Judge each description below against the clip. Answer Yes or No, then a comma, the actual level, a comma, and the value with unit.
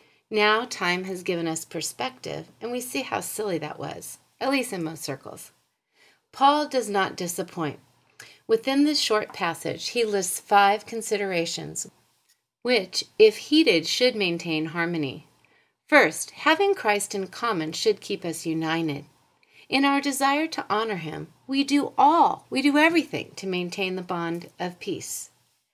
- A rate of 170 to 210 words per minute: No, average, 145 wpm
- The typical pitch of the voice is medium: No, high, 195 Hz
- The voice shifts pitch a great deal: Yes, wide, 7.1 semitones